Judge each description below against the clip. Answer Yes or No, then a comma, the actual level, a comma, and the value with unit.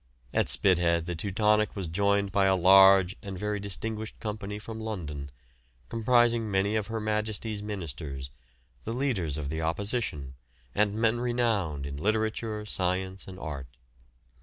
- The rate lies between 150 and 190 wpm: No, average, 140 wpm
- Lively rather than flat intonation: No, average, 3.7 semitones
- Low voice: Yes, low, 100 Hz